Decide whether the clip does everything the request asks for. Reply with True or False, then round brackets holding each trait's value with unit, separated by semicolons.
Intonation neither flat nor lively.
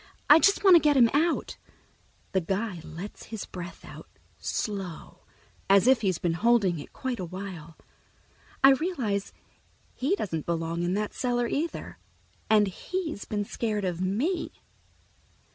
False (6.4 semitones)